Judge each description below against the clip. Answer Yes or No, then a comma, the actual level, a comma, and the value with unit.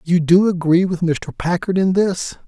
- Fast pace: No, average, 195 wpm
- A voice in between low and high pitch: Yes, medium, 180 Hz